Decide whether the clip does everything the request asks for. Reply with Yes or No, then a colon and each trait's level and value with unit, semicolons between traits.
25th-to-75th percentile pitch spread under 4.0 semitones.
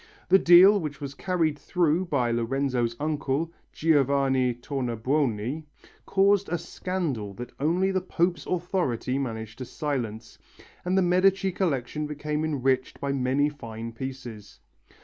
No: wide, 5.5 semitones